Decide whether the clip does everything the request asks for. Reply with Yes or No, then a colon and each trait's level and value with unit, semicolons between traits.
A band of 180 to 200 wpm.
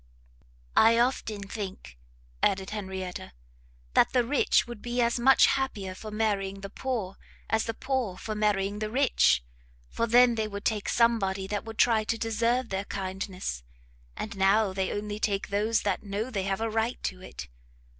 No: average, 170 wpm